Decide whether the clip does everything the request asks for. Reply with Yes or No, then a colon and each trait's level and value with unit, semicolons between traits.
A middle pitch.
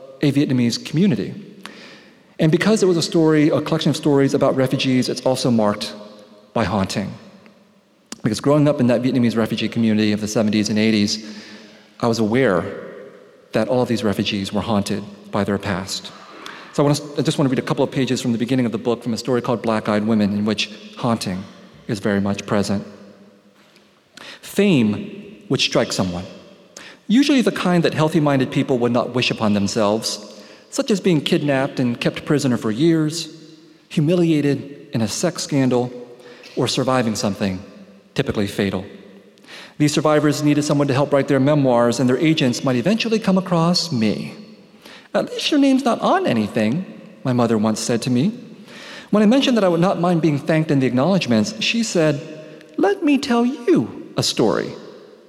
No: low, 130 Hz